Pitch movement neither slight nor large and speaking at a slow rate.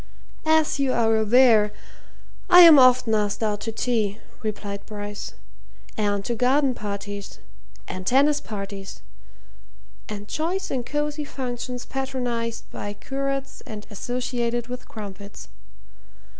Yes: average, 4.3 semitones; slow, 115 wpm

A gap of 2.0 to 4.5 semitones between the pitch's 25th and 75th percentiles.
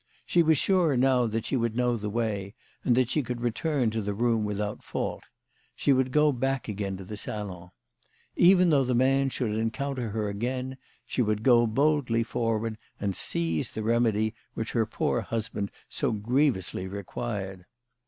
Yes: average, 3.7 semitones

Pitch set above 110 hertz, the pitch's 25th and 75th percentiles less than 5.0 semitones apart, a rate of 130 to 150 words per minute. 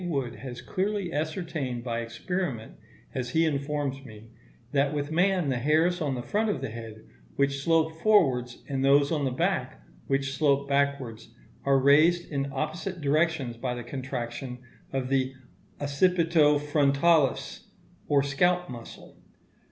Yes: medium, 140 Hz; average, 3.6 semitones; average, 145 wpm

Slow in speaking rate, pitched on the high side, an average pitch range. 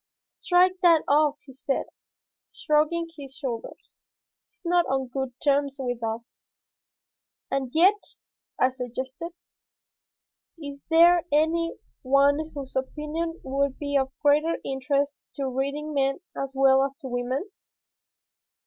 Yes: slow, 125 wpm; very high, 280 Hz; average, 3.1 semitones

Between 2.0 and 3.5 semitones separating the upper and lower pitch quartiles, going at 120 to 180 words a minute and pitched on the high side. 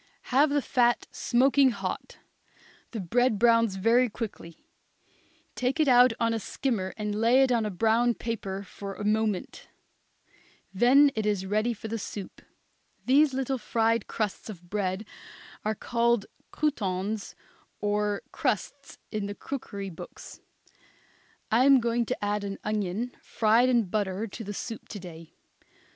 Yes: average, 3.2 semitones; average, 145 wpm; high, 220 Hz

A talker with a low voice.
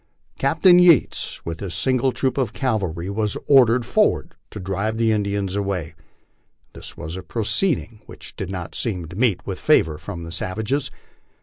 Yes: low, 105 Hz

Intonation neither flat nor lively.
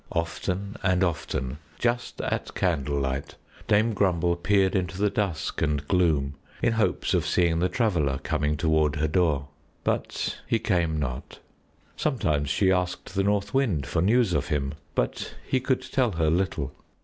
Yes: average, 5.0 semitones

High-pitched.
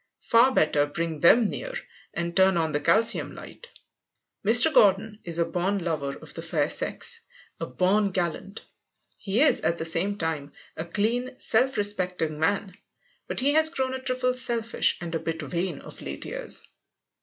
Yes: high, 195 Hz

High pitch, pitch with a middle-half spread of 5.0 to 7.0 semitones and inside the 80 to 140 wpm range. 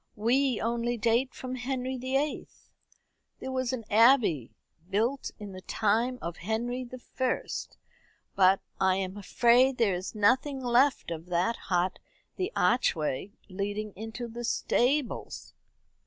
No: high, 235 Hz; average, 4.3 semitones; slow, 135 wpm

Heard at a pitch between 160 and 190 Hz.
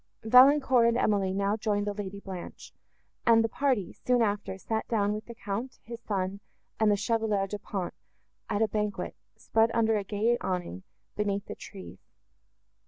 No: high, 210 Hz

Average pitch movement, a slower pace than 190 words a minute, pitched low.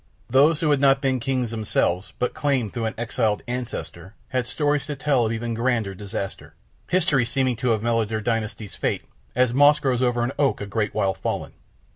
No: average, 3.4 semitones; average, 195 wpm; low, 120 Hz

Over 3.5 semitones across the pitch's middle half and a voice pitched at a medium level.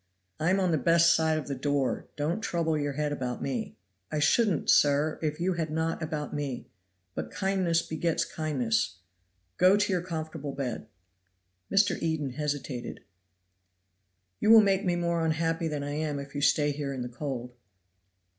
No: average, 2.9 semitones; medium, 155 Hz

